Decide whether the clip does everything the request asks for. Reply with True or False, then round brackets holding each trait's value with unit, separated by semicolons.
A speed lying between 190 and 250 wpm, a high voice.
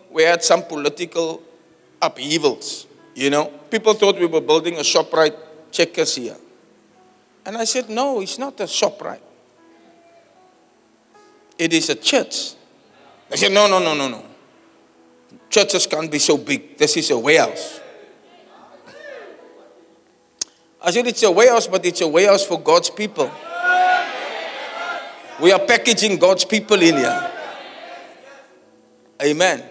False (135 wpm; 205 Hz)